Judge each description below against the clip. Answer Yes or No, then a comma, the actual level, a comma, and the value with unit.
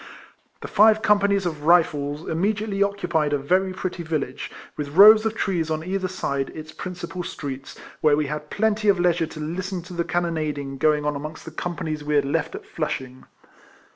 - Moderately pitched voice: Yes, medium, 165 Hz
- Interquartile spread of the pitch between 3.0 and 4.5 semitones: Yes, average, 4.1 semitones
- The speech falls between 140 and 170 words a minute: No, average, 190 wpm